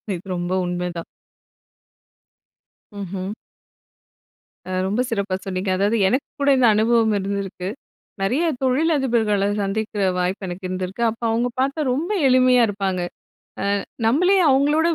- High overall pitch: Yes, high, 210 Hz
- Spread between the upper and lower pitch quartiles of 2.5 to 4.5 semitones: No, average, 5.1 semitones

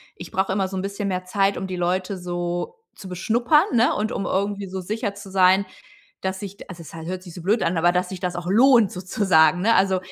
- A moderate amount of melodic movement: No, narrow, 1.9 semitones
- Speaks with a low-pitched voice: No, high, 190 Hz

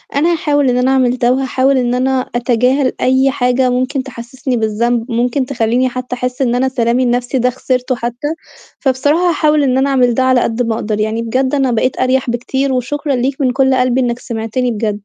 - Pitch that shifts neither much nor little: No, narrow, 1.6 semitones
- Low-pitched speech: No, very high, 255 Hz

